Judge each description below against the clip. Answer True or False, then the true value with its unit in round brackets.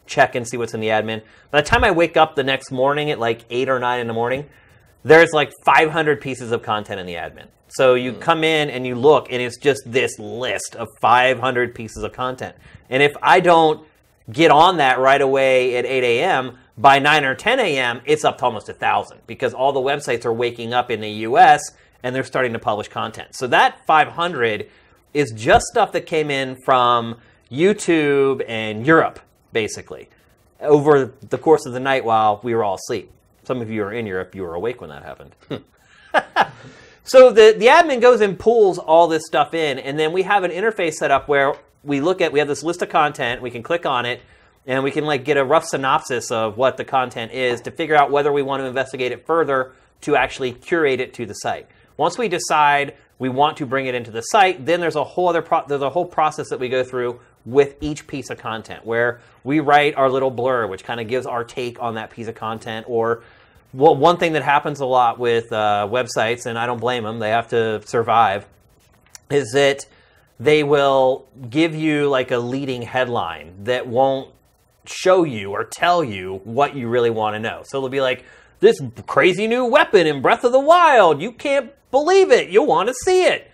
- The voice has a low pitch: True (130 Hz)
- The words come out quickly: True (215 wpm)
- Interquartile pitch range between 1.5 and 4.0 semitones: False (4.4 semitones)